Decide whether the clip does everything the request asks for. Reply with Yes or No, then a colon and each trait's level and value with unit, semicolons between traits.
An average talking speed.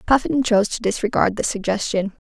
Yes: average, 160 wpm